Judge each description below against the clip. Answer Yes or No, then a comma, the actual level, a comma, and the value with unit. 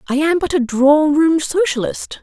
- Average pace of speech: Yes, average, 190 wpm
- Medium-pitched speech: No, very high, 300 Hz